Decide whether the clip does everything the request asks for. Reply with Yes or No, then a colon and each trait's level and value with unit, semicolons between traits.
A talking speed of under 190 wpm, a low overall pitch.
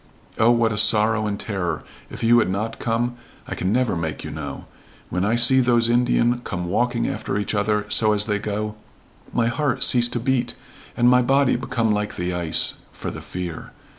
No: average, 195 wpm; low, 110 Hz